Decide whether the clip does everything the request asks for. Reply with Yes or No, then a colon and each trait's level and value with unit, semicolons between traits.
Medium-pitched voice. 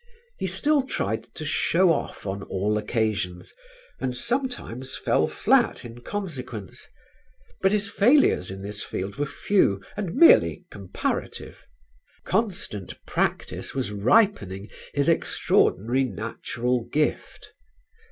No: low, 125 Hz